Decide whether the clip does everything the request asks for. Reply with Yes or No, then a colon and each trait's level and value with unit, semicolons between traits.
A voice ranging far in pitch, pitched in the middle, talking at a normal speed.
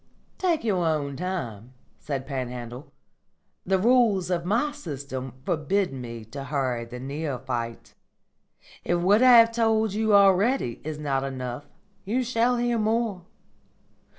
No: wide, 8.9 semitones; medium, 170 Hz; slow, 130 wpm